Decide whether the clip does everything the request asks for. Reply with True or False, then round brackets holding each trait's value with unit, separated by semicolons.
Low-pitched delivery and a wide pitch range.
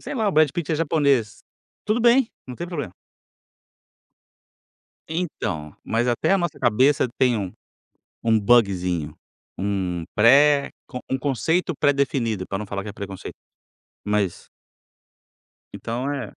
True (125 Hz; 6.7 semitones)